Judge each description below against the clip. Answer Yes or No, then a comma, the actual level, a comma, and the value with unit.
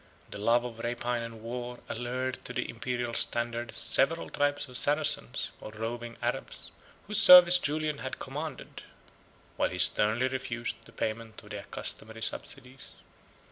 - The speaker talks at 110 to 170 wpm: Yes, average, 145 wpm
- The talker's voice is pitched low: Yes, low, 120 Hz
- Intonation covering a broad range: No, narrow, 2.6 semitones